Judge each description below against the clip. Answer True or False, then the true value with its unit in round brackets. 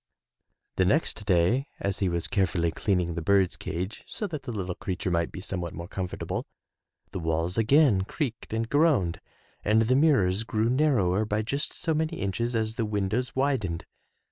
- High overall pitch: False (105 Hz)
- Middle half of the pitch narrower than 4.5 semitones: False (5.6 semitones)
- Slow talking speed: False (175 wpm)